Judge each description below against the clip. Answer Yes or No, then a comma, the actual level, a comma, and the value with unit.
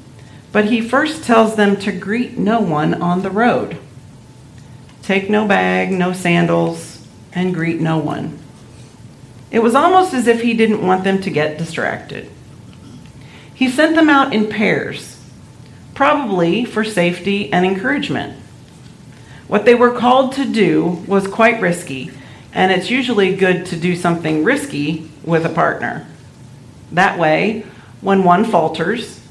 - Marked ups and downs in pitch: Yes, wide, 6.2 semitones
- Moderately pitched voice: Yes, medium, 180 Hz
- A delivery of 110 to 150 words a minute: Yes, average, 140 wpm